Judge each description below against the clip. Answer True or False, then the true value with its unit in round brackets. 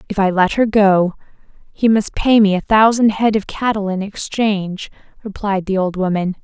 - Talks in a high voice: True (200 Hz)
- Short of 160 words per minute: False (185 wpm)